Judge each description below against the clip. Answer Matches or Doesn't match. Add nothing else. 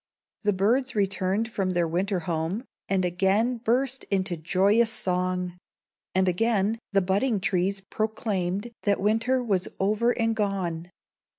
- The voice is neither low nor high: Doesn't match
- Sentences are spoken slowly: Matches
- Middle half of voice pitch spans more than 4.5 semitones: Doesn't match